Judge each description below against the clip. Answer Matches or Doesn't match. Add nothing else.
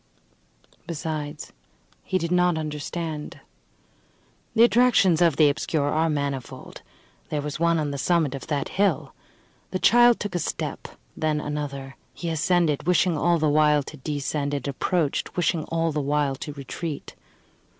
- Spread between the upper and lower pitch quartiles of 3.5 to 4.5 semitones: Doesn't match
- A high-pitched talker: Doesn't match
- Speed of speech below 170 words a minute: Matches